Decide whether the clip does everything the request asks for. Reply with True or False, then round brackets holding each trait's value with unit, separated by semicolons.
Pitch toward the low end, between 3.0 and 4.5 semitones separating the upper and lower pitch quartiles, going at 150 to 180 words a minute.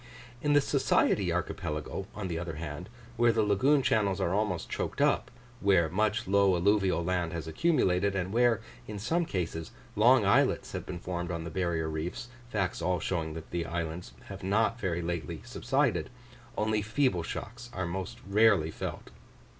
True (95 Hz; 4.1 semitones; 170 wpm)